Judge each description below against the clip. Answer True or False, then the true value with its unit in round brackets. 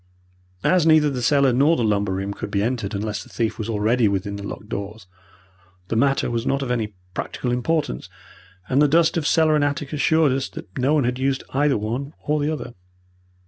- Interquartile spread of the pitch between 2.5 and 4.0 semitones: False (5.4 semitones)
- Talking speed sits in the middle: False (210 wpm)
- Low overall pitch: True (125 Hz)